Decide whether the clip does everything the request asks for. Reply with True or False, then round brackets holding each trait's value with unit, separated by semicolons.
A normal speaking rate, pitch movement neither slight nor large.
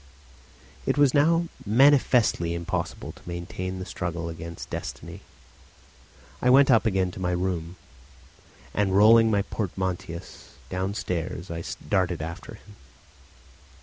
False (115 wpm; 4.2 semitones)